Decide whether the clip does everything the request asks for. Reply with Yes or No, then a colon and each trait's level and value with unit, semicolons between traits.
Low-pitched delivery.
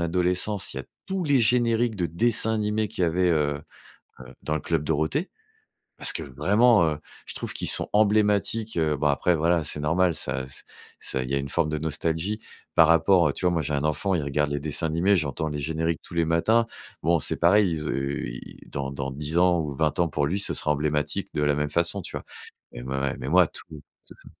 Yes: very low, 80 Hz